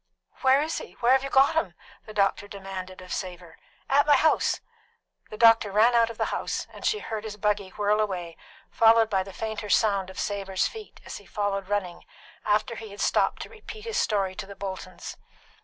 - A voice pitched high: Yes, high, 210 Hz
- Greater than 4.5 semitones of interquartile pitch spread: No, average, 3.2 semitones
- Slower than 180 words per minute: No, fast, 205 wpm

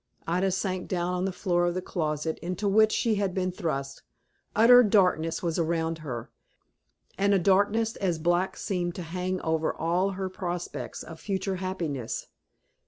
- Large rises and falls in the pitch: No, average, 2.8 semitones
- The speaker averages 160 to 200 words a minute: Yes, average, 165 wpm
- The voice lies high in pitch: No, medium, 180 Hz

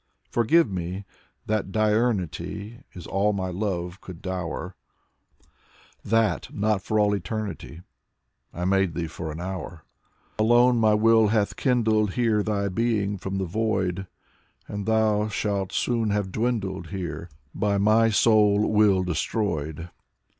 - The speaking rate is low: Yes, slow, 130 wpm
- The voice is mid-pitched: No, low, 100 Hz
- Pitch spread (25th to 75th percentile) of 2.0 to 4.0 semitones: Yes, average, 2.8 semitones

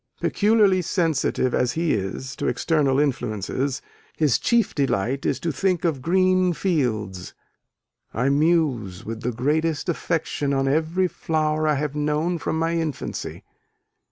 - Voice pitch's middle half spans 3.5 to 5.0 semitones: Yes, average, 4.2 semitones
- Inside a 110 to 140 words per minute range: Yes, slow, 135 wpm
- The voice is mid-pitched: Yes, medium, 150 Hz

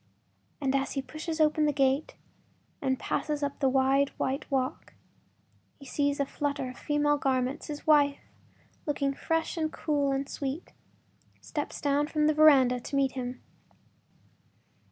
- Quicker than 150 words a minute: No, average, 145 wpm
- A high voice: Yes, very high, 280 Hz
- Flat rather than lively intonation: Yes, narrow, 1.9 semitones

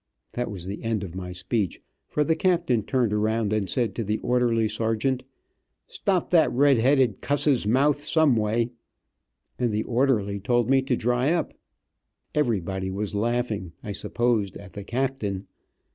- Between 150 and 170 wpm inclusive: Yes, average, 160 wpm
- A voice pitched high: No, low, 115 Hz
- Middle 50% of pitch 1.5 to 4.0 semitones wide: No, average, 4.4 semitones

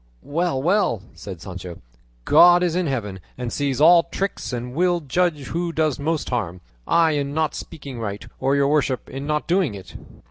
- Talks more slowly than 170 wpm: No, average, 180 wpm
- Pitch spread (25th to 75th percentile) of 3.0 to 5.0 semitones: No, wide, 5.4 semitones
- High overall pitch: No, medium, 145 Hz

